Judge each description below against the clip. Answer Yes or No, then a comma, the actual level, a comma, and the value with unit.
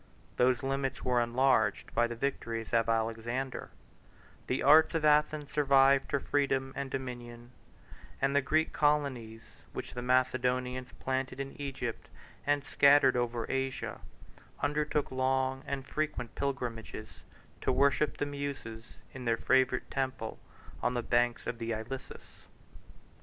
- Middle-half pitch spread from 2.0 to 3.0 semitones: Yes, narrow, 2.6 semitones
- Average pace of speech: No, slow, 130 wpm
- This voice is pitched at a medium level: No, low, 130 Hz